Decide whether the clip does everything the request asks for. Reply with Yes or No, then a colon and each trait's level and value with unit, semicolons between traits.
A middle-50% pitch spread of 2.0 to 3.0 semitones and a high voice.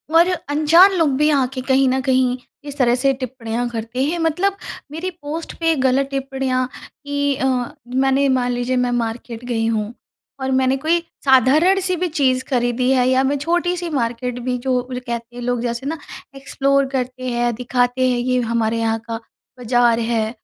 Yes: narrow, 2.5 semitones; very high, 255 Hz